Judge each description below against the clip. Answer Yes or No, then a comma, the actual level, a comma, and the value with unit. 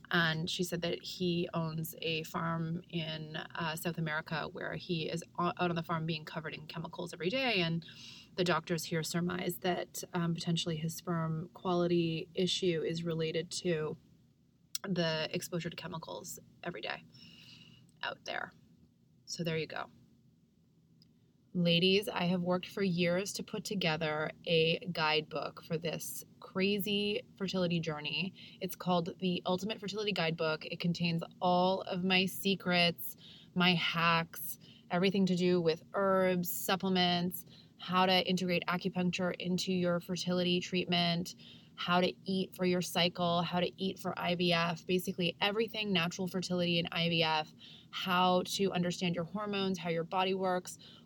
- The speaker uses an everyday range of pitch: No, narrow, 1.8 semitones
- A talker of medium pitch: Yes, medium, 175 Hz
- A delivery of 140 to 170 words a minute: Yes, average, 145 wpm